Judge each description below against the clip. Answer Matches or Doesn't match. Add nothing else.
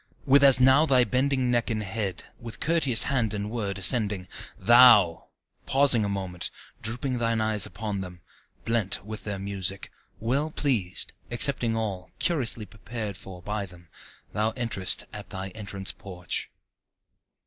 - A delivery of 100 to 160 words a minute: Matches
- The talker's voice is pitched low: Matches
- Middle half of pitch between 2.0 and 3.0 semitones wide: Doesn't match